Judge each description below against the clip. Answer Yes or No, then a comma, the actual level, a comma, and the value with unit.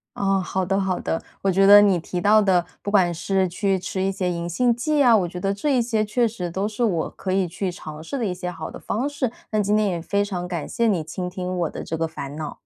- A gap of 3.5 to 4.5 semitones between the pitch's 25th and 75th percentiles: No, average, 3.1 semitones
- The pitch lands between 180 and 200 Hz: Yes, high, 190 Hz